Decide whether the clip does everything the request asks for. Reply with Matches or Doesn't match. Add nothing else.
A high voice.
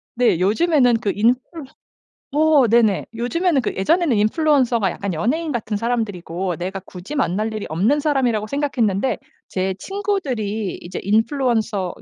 Matches